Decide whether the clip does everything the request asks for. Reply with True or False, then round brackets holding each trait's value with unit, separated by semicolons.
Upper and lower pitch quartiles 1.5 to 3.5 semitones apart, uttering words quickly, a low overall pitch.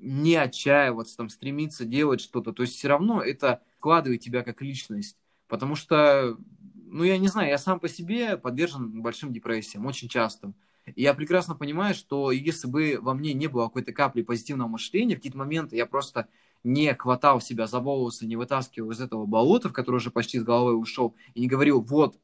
False (4.1 semitones; 190 wpm; 130 Hz)